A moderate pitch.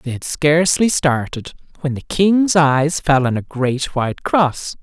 Yes: medium, 150 Hz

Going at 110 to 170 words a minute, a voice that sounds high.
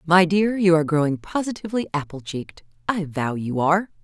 No: average, 165 wpm; medium, 170 Hz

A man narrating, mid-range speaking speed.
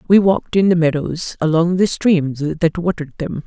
No: female; average, 190 wpm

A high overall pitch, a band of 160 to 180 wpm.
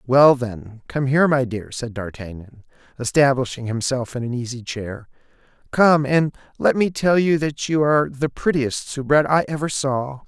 No: low, 135 Hz; average, 170 wpm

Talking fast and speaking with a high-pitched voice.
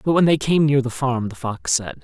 No: fast, 295 wpm; low, 130 Hz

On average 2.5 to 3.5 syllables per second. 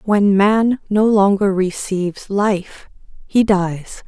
Yes: 3.1 syllables/s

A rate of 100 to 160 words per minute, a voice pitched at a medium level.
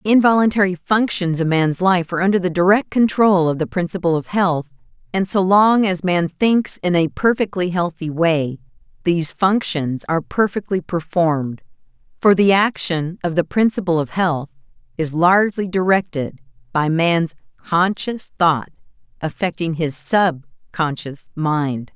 Yes: average, 140 wpm; medium, 175 Hz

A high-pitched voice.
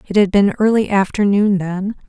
Yes: high, 200 Hz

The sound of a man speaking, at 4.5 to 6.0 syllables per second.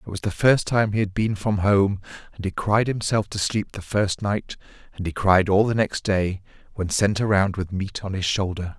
Yes: male; 4.9 syllables/s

